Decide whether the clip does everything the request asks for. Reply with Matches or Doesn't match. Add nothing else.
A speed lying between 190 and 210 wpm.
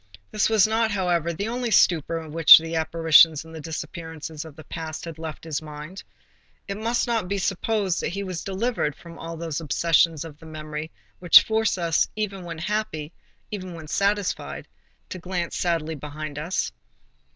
Doesn't match